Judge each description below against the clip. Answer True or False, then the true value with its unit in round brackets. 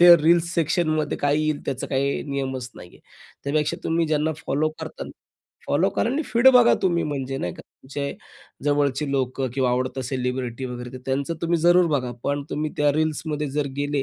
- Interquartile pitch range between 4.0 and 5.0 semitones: False (3.0 semitones)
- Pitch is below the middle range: False (145 Hz)